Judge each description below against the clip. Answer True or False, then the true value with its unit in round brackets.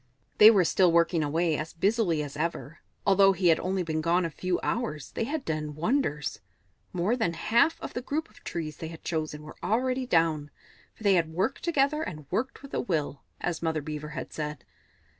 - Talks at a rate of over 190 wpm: True (200 wpm)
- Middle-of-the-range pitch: True (170 Hz)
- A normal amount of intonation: False (6.1 semitones)